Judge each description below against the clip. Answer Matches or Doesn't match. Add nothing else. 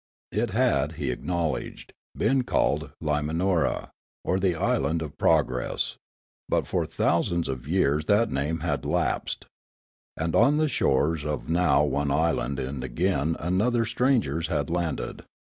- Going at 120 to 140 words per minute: Matches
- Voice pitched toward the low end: Matches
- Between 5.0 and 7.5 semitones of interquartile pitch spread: Doesn't match